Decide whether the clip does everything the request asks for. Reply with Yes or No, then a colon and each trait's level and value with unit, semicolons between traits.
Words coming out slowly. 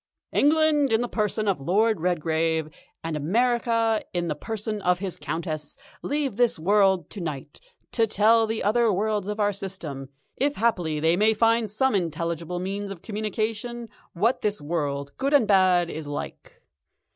No: average, 160 wpm